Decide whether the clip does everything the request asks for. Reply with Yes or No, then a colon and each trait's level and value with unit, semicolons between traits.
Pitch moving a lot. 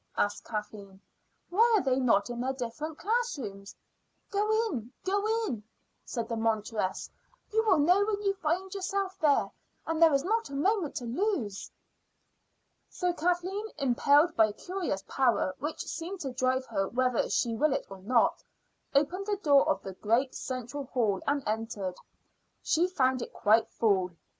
Yes: wide, 8.2 semitones